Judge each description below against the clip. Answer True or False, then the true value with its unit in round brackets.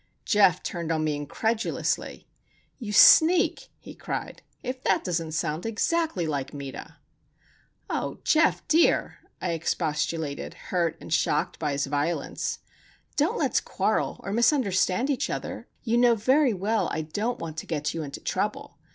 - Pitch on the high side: False (180 Hz)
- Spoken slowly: False (145 wpm)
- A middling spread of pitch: False (7.1 semitones)